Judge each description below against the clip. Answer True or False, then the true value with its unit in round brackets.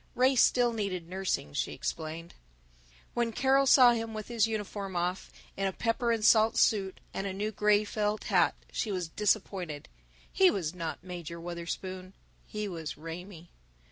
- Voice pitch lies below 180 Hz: False (195 Hz)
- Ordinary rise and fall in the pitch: True (4.0 semitones)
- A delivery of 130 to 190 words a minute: True (160 wpm)